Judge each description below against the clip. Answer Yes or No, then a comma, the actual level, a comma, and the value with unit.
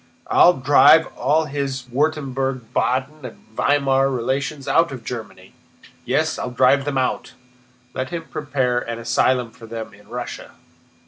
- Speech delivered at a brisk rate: No, average, 140 wpm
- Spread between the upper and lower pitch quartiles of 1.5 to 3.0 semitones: Yes, average, 2.7 semitones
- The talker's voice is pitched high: No, low, 130 Hz